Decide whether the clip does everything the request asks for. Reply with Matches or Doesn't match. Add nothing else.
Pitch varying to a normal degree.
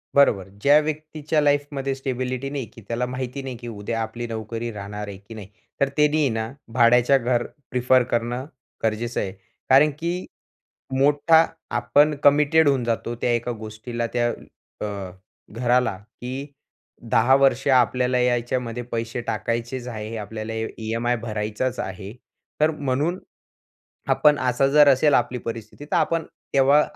Matches